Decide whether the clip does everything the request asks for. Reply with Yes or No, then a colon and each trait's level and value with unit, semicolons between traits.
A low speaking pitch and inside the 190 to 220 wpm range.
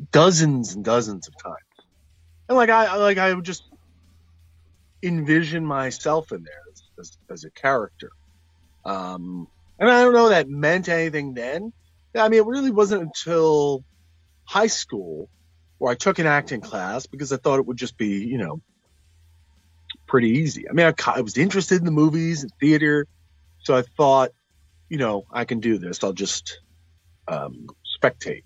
No: low, 125 Hz; average, 170 wpm